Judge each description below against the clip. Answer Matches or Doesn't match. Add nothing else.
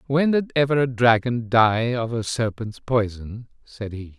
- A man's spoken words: Matches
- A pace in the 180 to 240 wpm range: Doesn't match